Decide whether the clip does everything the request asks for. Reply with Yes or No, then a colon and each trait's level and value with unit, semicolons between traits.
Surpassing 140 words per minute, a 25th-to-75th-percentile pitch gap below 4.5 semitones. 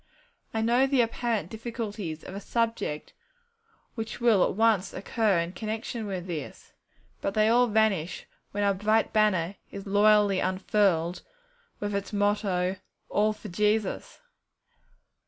No: slow, 135 wpm; average, 2.8 semitones